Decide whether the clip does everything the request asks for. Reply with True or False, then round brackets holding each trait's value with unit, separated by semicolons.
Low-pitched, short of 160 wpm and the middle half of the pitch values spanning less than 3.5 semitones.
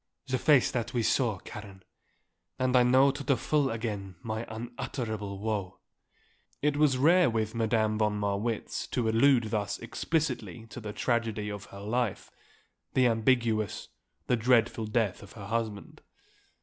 True (115 Hz; 150 wpm; 3.1 semitones)